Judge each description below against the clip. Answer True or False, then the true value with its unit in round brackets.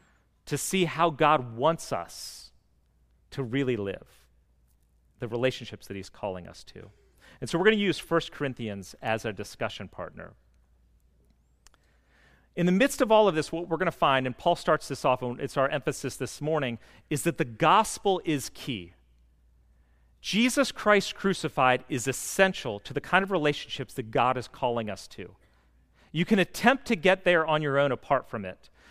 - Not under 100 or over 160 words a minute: False (175 wpm)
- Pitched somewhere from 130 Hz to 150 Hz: True (135 Hz)